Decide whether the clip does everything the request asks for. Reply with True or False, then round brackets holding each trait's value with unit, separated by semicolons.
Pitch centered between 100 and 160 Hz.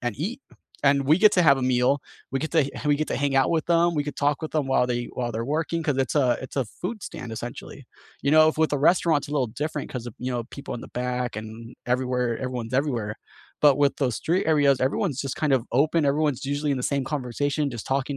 True (140 Hz)